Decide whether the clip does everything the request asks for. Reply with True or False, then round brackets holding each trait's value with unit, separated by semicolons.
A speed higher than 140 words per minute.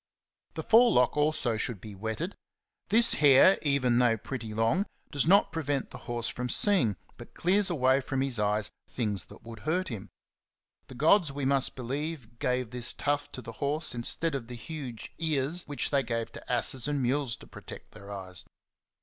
True (180 wpm)